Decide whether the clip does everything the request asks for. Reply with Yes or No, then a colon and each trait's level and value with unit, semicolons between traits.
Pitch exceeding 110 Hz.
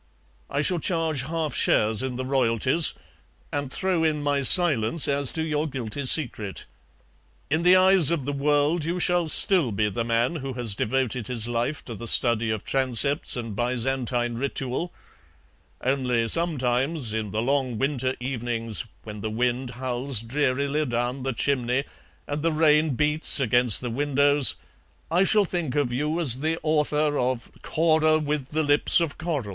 Yes: low, 135 Hz